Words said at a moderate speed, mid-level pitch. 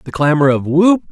No: fast, 215 wpm; medium, 160 Hz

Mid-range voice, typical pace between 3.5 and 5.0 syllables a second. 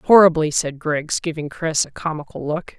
Yes: medium, 160 Hz; 4.7 syllables/s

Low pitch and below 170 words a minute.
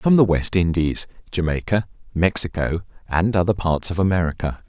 Yes: very low, 90 Hz; average, 140 wpm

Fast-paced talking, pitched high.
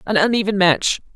No: average, 155 wpm; high, 200 Hz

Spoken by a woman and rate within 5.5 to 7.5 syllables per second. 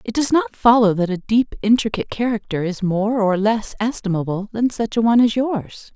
No: female; 5.3 syllables/s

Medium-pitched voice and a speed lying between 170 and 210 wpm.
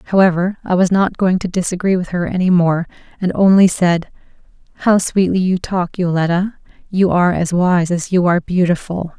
Yes: medium, 180 Hz; average, 175 wpm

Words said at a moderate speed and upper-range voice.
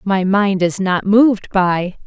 Yes: average, 175 wpm; high, 195 Hz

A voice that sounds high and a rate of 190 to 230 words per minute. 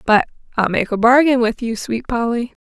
Yes: high, 235 Hz; fast, 205 wpm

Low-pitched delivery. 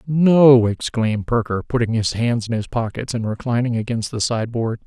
Yes: low, 120 Hz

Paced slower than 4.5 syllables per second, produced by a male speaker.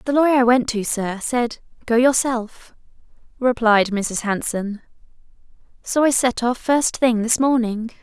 No: 4.2 syllables/s; female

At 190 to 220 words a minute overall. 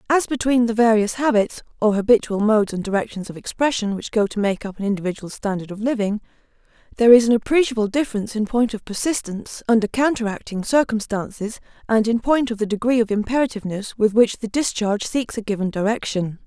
No: average, 180 wpm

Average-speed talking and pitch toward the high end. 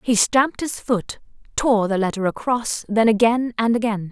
Yes: average, 175 wpm; high, 225 Hz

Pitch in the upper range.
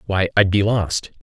No: low, 100 Hz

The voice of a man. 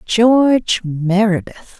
No: female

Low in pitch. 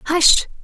No: very high, 330 Hz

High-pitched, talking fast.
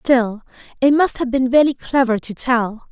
No: very high, 250 Hz; average, 185 wpm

